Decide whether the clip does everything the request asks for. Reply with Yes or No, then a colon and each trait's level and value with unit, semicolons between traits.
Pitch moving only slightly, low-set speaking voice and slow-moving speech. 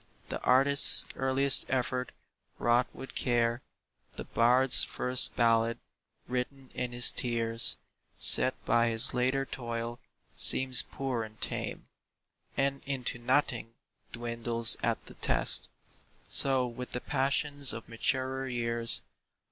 Yes: narrow, 2.1 semitones; low, 125 Hz; slow, 115 wpm